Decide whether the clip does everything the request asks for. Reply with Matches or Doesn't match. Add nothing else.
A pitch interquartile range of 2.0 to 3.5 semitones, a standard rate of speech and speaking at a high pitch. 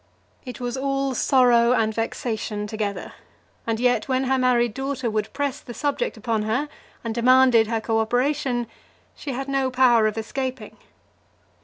Matches